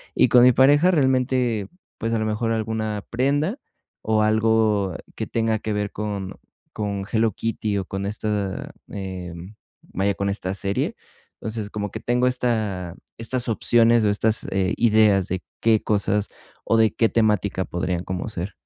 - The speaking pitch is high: No, low, 110 Hz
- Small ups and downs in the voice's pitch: Yes, narrow, 2.3 semitones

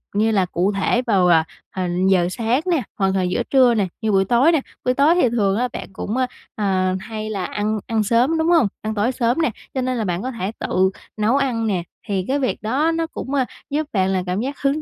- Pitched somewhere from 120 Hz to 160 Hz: No, high, 225 Hz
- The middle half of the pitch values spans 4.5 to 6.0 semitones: Yes, average, 5.2 semitones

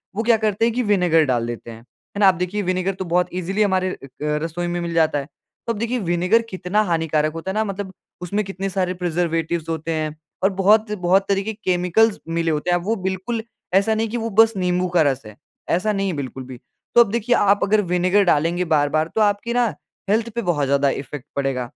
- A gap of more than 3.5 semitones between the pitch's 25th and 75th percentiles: Yes, average, 4.3 semitones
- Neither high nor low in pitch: Yes, medium, 180 Hz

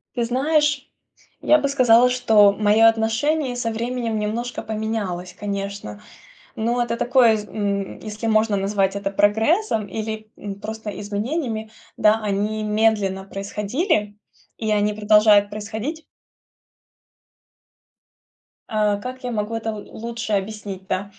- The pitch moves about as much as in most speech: No, narrow, 2.3 semitones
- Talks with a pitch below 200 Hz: No, high, 215 Hz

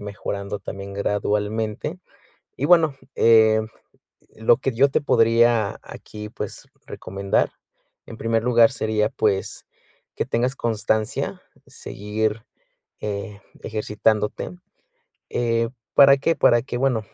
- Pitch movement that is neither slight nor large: No, narrow, 2.1 semitones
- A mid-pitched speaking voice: No, low, 110 Hz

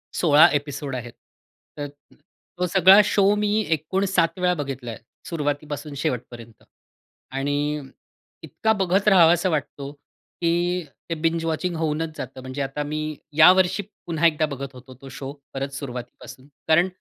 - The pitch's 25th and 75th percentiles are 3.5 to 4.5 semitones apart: Yes, average, 4.1 semitones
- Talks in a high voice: No, medium, 155 Hz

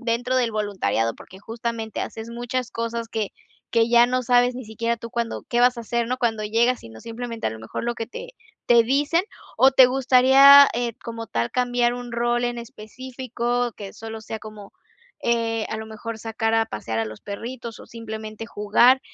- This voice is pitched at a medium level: No, high, 235 Hz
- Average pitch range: No, narrow, 1.9 semitones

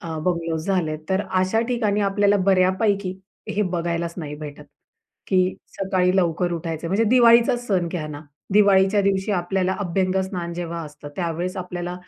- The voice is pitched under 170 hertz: No, medium, 185 Hz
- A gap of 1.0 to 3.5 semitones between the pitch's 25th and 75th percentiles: Yes, narrow, 2.6 semitones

